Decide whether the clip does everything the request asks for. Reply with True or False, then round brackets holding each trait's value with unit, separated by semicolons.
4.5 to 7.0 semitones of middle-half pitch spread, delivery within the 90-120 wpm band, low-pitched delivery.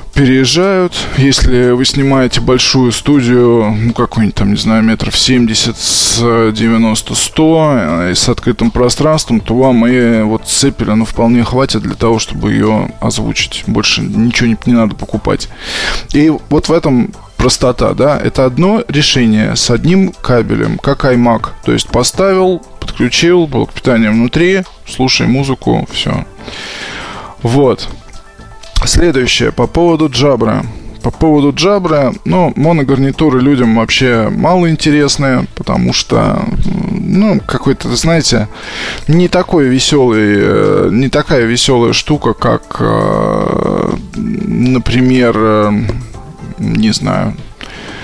True (5.4 semitones; 115 wpm; 130 Hz)